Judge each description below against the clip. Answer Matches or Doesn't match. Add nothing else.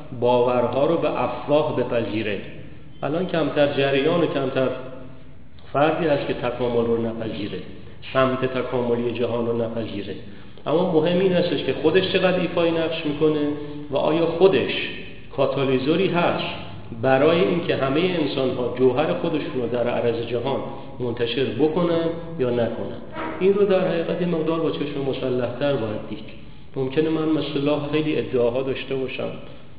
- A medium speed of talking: Matches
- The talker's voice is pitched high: Doesn't match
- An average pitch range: Matches